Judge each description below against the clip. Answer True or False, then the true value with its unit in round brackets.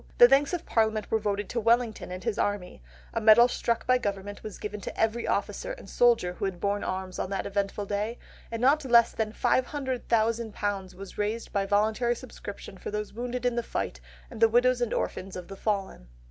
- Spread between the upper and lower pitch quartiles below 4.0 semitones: True (3.0 semitones)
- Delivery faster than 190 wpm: True (200 wpm)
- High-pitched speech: True (220 Hz)